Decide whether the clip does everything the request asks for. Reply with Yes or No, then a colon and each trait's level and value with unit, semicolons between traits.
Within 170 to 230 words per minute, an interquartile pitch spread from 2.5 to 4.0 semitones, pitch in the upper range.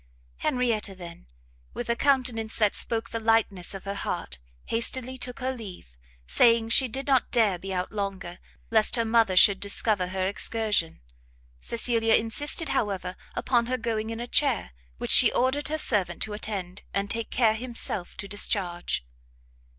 No: average, 160 wpm; average, 3.6 semitones; high, 220 Hz